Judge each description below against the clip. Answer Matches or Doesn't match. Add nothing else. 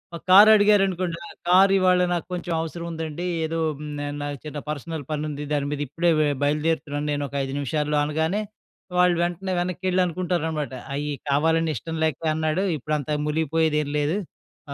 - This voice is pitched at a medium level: Matches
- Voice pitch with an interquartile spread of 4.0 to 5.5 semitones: Doesn't match